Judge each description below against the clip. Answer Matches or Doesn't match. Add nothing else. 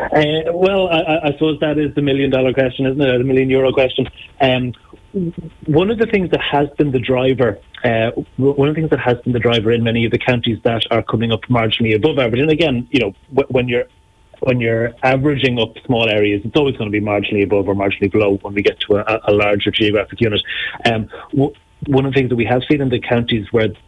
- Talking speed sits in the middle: Doesn't match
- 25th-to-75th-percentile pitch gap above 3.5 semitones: Matches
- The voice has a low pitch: Matches